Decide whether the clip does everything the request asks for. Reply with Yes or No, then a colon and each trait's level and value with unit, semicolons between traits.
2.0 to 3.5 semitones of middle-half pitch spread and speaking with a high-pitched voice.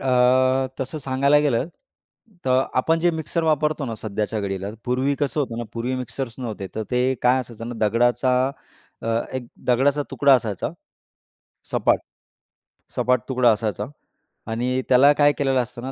No: average, 3.1 semitones; low, 125 Hz